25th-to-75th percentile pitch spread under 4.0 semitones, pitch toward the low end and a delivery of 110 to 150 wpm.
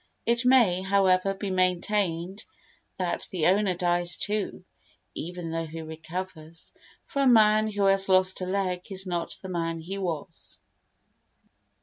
No: narrow, 2.4 semitones; medium, 185 Hz; average, 140 wpm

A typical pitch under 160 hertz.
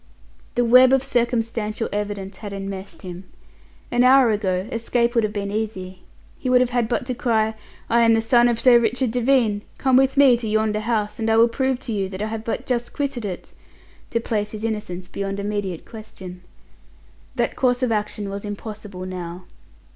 No: high, 220 Hz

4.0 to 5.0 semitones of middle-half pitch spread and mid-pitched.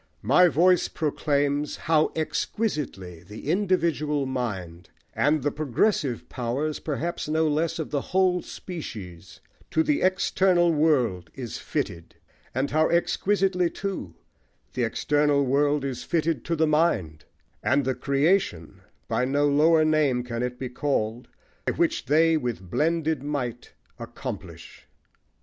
Yes: average, 4.6 semitones; medium, 145 Hz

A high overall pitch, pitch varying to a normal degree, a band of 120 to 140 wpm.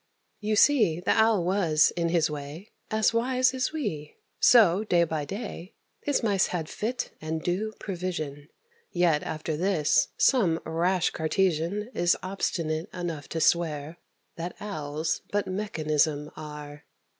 No: medium, 175 Hz; average, 4.7 semitones; slow, 135 wpm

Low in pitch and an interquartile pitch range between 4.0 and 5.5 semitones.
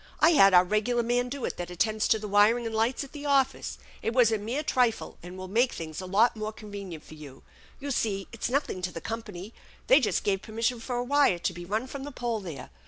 No: high, 220 Hz; average, 4.4 semitones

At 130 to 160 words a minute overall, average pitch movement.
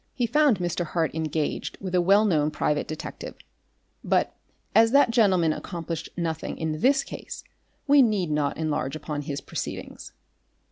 No: average, 150 wpm; wide, 5.7 semitones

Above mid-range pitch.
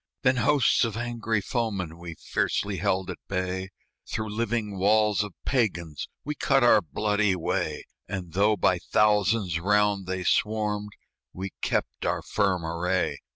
No: low, 105 Hz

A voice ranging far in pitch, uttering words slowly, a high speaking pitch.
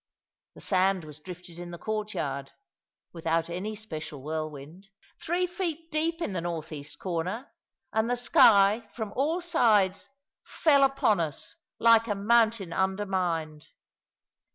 Yes: wide, 5.9 semitones; slow, 130 wpm; high, 195 Hz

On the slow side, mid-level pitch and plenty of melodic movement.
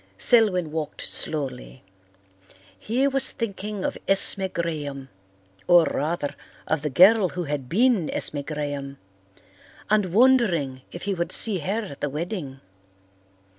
Yes: slow, 130 wpm; medium, 170 Hz; wide, 6.0 semitones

